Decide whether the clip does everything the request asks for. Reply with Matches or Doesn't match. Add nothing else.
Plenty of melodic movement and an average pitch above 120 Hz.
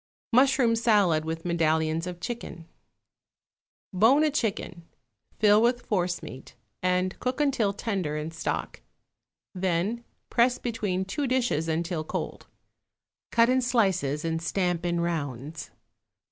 Matches